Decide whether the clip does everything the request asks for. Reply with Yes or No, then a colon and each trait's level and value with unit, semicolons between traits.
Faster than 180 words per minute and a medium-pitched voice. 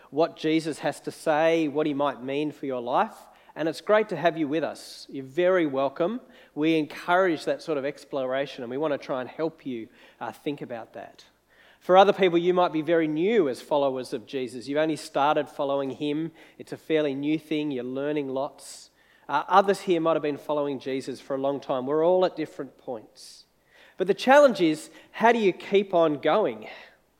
Yes: fast, 205 wpm; medium, 155 Hz